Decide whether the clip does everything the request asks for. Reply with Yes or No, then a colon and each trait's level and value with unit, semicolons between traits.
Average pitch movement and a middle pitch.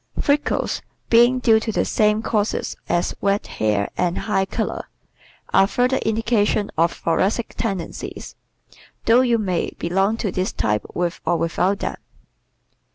No: average, 4.2 semitones; high, 205 Hz